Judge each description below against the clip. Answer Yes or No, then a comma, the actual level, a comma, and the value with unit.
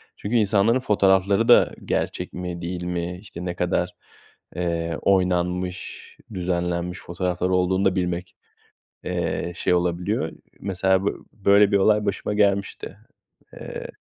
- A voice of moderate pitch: No, very low, 90 Hz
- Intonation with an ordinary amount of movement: No, narrow, 2.0 semitones